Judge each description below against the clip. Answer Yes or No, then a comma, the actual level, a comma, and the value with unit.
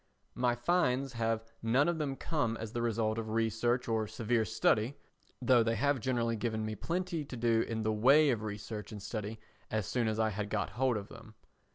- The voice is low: Yes, low, 115 Hz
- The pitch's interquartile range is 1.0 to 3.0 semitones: Yes, narrow, 2.5 semitones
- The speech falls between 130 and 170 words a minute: No, fast, 205 wpm